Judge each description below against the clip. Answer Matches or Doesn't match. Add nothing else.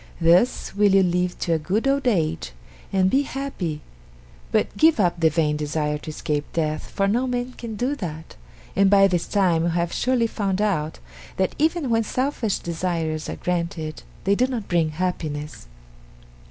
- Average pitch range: Doesn't match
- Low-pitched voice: Doesn't match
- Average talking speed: Matches